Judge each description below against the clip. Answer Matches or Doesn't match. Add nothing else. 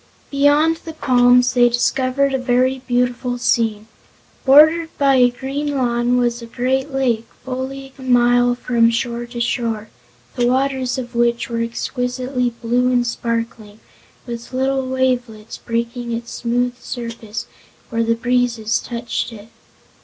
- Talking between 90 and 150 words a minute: Matches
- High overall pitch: Matches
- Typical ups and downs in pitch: Doesn't match